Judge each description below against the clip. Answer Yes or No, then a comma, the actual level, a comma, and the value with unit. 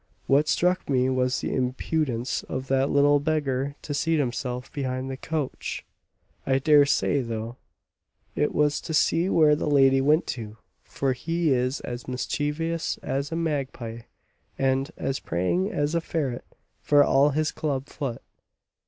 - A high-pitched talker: No, medium, 140 Hz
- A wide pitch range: No, average, 2.8 semitones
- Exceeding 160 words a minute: No, average, 155 wpm